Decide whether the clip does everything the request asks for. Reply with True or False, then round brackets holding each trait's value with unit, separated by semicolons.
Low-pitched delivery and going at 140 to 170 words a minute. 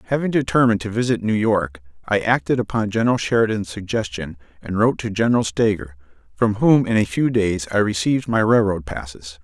False (105 Hz; 180 wpm)